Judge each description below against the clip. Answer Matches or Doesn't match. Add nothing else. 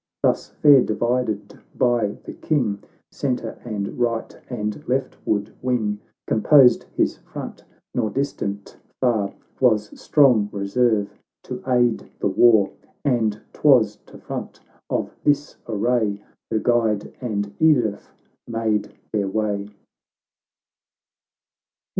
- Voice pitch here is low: Matches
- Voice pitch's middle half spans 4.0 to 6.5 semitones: Doesn't match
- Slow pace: Matches